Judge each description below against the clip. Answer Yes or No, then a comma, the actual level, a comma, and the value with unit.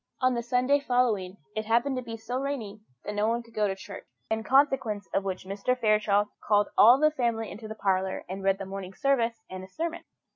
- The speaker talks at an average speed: No, fast, 215 wpm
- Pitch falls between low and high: No, high, 220 Hz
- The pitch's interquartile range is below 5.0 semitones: Yes, average, 3.9 semitones